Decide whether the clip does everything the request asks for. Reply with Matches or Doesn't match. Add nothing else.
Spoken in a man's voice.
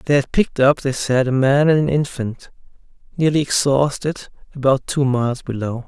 Matches